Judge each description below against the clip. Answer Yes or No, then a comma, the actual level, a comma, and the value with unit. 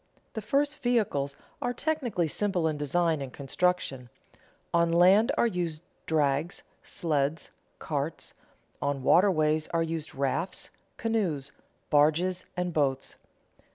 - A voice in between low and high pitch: Yes, medium, 165 Hz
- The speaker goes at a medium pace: No, slow, 115 wpm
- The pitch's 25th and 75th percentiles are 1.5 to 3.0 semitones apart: No, average, 4.2 semitones